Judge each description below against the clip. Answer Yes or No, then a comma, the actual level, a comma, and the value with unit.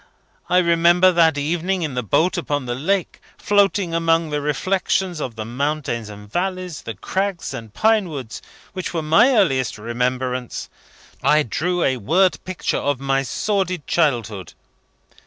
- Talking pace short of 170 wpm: Yes, average, 150 wpm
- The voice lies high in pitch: No, medium, 160 Hz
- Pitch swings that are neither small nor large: No, wide, 6.1 semitones